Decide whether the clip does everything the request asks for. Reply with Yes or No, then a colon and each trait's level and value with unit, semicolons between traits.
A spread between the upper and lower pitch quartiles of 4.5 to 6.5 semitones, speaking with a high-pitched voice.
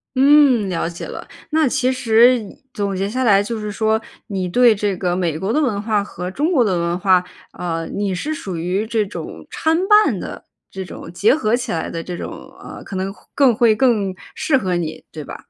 Yes: average, 5.2 semitones; high, 205 Hz